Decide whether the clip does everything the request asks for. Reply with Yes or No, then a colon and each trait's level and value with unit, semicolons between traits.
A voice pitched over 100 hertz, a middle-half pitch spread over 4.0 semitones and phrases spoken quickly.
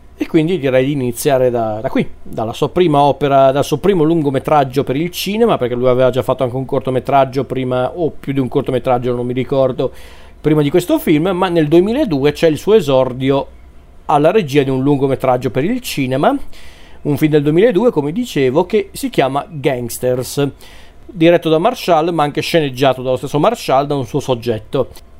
No: medium, 140 Hz; average, 3.7 semitones; fast, 185 wpm